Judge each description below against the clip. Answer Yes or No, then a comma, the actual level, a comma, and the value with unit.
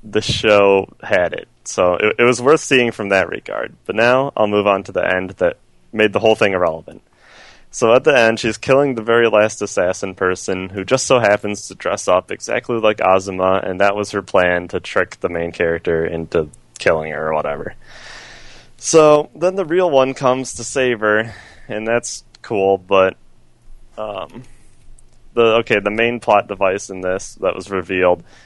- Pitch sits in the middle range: No, low, 105 Hz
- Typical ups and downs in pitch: Yes, average, 3.9 semitones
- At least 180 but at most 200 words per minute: Yes, average, 185 wpm